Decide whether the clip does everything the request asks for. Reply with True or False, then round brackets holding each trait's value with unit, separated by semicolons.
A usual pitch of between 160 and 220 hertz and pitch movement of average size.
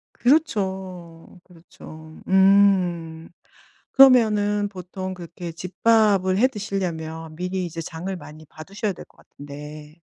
True (185 Hz; 3.6 semitones)